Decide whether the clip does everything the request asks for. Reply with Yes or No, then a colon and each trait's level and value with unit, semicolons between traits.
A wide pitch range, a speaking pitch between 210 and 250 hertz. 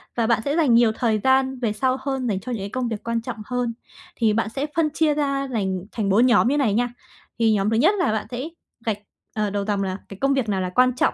No: average, 3.8 semitones; high, 235 Hz